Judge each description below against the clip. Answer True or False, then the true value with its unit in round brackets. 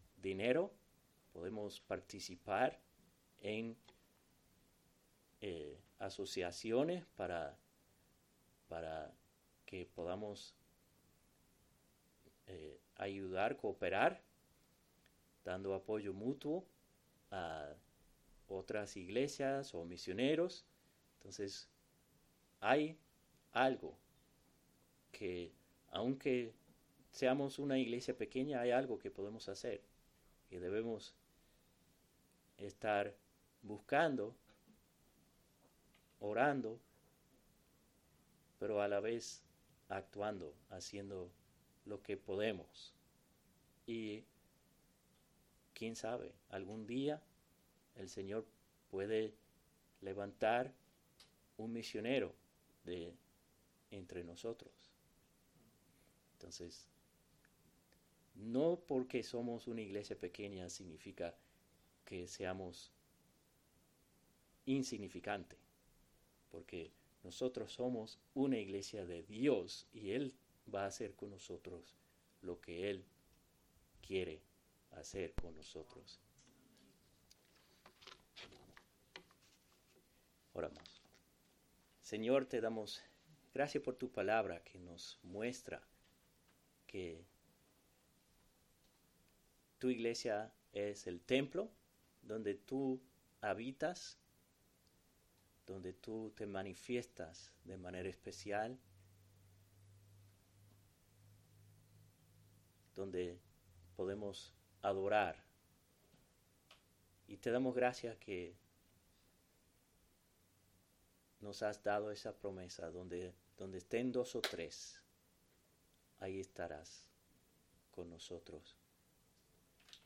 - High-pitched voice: False (100 Hz)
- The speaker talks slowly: True (70 wpm)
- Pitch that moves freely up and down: False (4.1 semitones)